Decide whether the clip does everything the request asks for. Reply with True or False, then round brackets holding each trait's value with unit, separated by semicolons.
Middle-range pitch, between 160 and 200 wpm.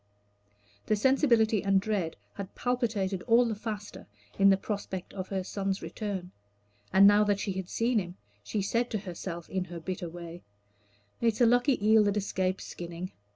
False (200 Hz; 175 wpm)